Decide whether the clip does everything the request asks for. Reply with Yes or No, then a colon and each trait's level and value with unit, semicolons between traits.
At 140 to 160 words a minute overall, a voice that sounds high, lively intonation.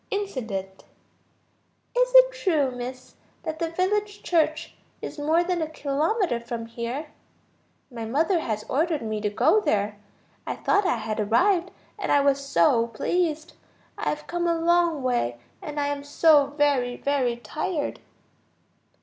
Yes: average, 150 wpm; very high, 290 Hz; wide, 6.3 semitones